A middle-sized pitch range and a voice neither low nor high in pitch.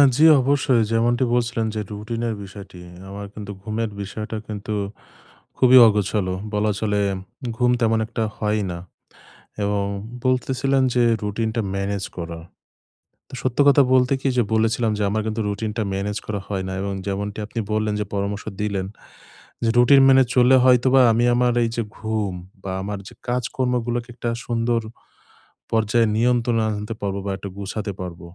No: average, 3.0 semitones; low, 110 Hz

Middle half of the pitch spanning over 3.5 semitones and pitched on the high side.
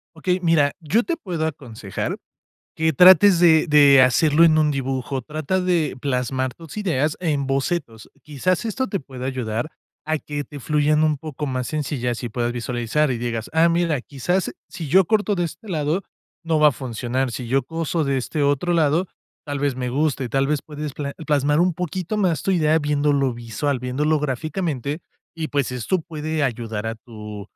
No: average, 4.0 semitones; medium, 150 Hz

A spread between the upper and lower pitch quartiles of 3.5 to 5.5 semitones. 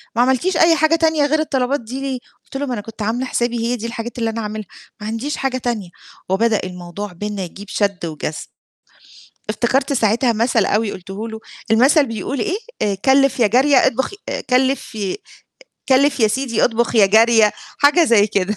Yes: average, 4.2 semitones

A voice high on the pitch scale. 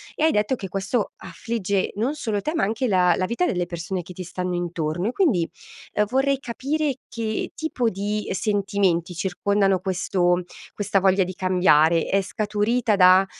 Yes: high, 195 Hz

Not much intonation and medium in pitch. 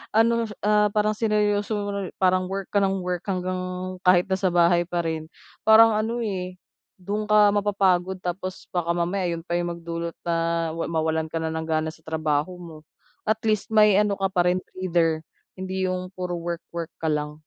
No: average, 3.3 semitones; medium, 180 Hz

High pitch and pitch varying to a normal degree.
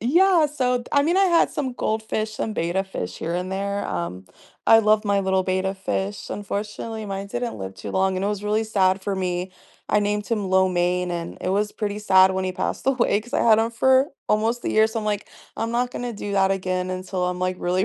Yes: high, 200 Hz; average, 3.0 semitones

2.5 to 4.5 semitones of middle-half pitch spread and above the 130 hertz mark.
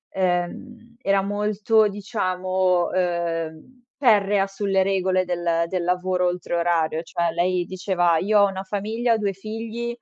Yes: average, 2.8 semitones; high, 190 Hz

